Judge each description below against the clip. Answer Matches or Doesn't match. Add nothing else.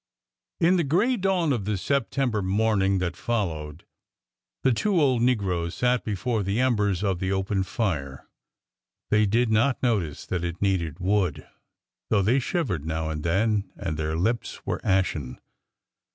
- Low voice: Matches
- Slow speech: Doesn't match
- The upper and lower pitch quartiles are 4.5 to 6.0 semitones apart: Matches